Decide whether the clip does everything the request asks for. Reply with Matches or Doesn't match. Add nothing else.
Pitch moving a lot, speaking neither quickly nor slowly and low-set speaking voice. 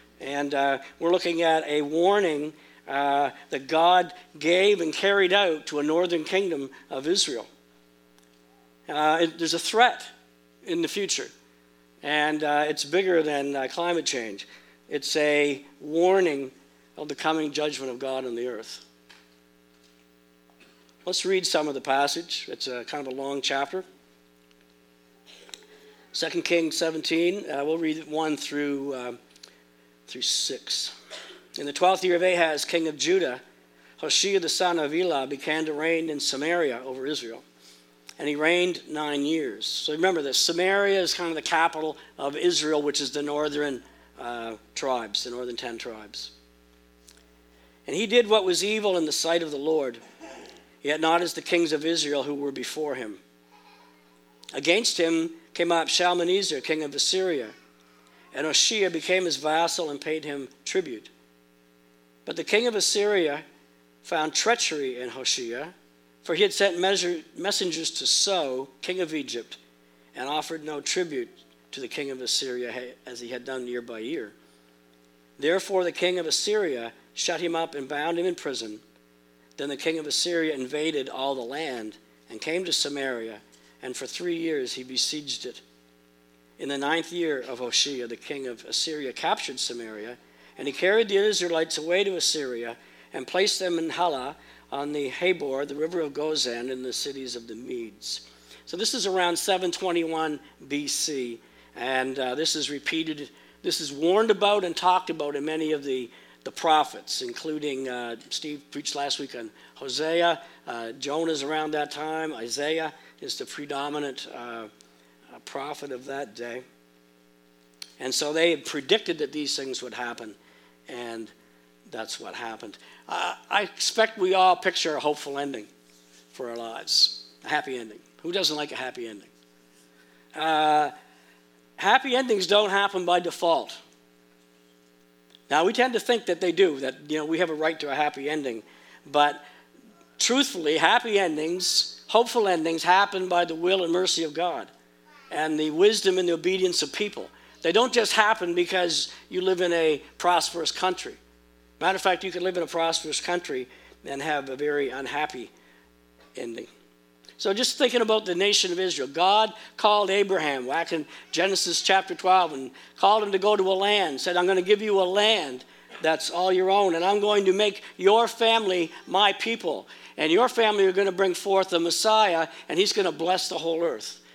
Doesn't match